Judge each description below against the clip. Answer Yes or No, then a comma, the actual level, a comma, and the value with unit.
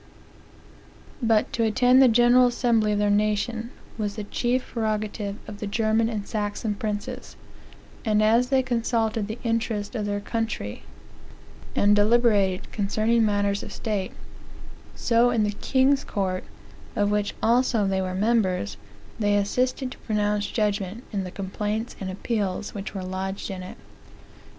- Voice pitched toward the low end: No, high, 215 Hz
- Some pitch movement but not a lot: No, narrow, 2.3 semitones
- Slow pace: No, average, 145 wpm